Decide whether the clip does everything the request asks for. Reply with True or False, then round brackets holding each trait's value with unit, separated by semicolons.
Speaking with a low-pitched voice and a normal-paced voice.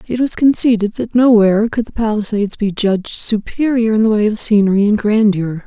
False (215 Hz; 190 wpm)